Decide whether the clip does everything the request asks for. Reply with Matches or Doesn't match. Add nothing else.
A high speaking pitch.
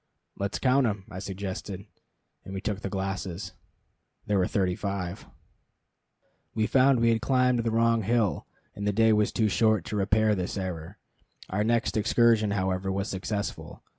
Doesn't match